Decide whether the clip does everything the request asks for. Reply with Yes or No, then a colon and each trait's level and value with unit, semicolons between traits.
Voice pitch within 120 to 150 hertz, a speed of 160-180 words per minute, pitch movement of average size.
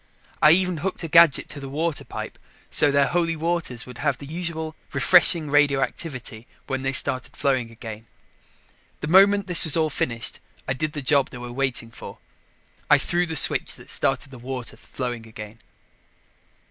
Yes: medium, 140 Hz; average, 170 wpm; average, 4.6 semitones